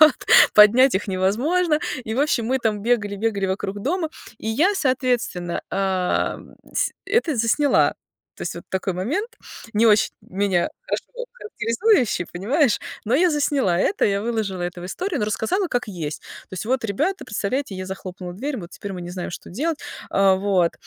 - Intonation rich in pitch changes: Yes, wide, 7.1 semitones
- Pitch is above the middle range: Yes, high, 220 Hz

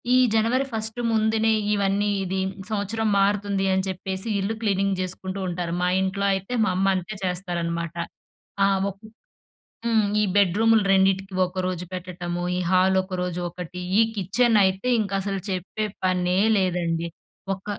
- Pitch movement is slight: Yes, narrow, 2.1 semitones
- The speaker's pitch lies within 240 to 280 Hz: No, high, 190 Hz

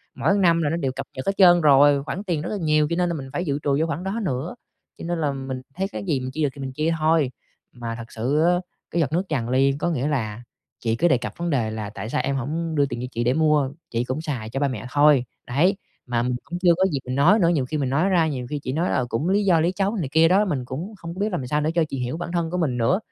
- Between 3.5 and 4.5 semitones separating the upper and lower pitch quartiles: No, average, 4.9 semitones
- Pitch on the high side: No, medium, 150 Hz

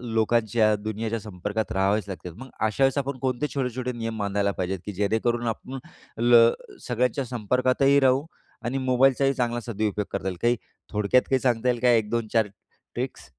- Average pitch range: Yes, average, 3.2 semitones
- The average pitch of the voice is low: Yes, low, 115 Hz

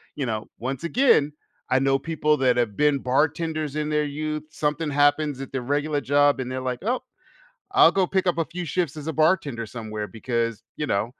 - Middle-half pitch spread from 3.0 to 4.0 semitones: Yes, average, 3.3 semitones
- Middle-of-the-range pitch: Yes, medium, 145 Hz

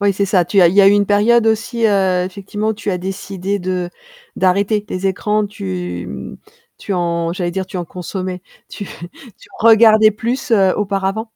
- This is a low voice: No, high, 195 Hz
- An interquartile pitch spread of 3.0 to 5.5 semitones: No, narrow, 2.6 semitones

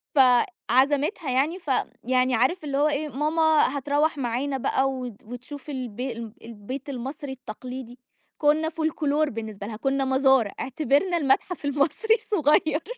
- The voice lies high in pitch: Yes, very high, 275 Hz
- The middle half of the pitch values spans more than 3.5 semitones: No, average, 3.2 semitones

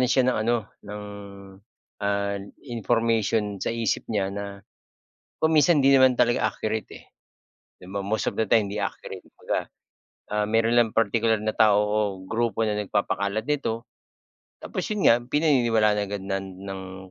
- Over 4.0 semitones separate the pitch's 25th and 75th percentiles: No, average, 2.8 semitones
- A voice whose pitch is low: Yes, low, 110 Hz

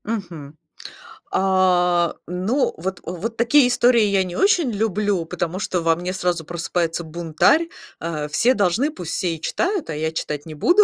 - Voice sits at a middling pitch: Yes, medium, 180 Hz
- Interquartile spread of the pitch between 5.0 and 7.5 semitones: Yes, average, 5.3 semitones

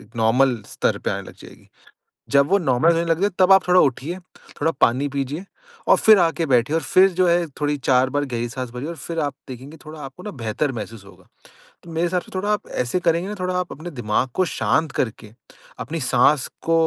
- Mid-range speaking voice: Yes, medium, 150 Hz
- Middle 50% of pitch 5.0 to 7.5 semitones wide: Yes, average, 5.3 semitones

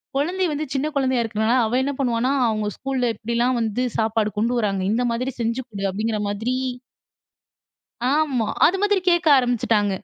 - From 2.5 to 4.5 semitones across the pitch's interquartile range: Yes, average, 3.6 semitones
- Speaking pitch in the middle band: No, high, 235 Hz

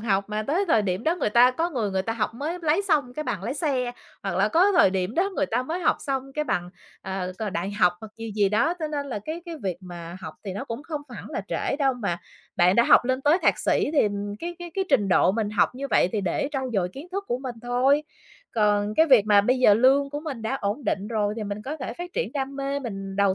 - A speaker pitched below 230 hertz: No, high, 240 Hz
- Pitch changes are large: Yes, wide, 5.9 semitones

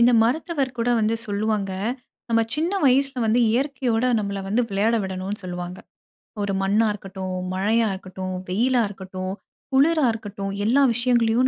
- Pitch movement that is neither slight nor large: Yes, average, 4.1 semitones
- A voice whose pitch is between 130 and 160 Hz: No, high, 220 Hz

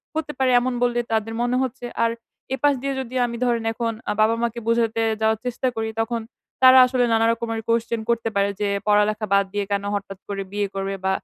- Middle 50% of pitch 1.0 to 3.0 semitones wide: Yes, narrow, 2.5 semitones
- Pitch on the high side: Yes, high, 230 Hz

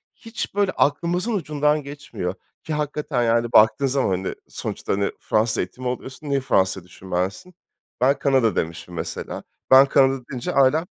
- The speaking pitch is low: Yes, low, 130 Hz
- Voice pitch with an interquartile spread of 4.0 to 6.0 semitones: Yes, wide, 5.5 semitones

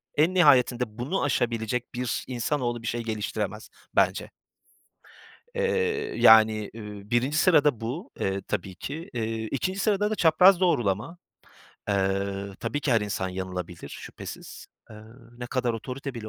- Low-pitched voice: Yes, low, 120 Hz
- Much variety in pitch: Yes, wide, 5.9 semitones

